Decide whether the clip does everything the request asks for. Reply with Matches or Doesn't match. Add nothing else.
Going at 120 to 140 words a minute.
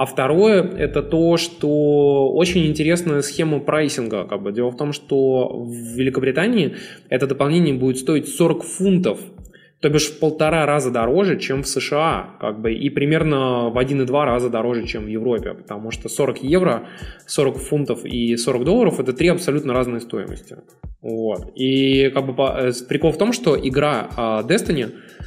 Doesn't match